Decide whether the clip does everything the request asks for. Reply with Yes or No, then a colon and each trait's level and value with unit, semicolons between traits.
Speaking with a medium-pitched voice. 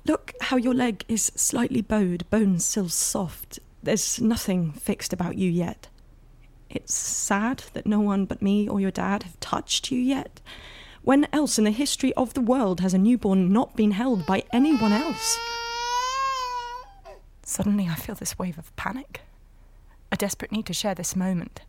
No: high, 220 Hz